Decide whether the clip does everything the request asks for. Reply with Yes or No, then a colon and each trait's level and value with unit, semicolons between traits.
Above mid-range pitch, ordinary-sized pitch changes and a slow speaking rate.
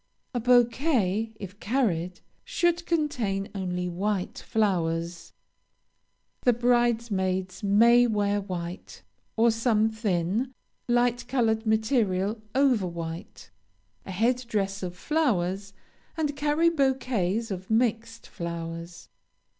Yes: high, 220 Hz; average, 4.7 semitones; slow, 100 wpm